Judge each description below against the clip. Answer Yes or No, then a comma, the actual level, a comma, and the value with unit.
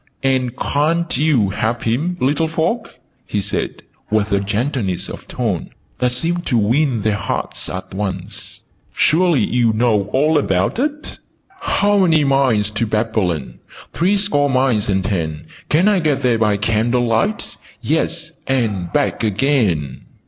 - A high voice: No, low, 120 Hz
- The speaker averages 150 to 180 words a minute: No, average, 140 wpm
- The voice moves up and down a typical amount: No, wide, 6.9 semitones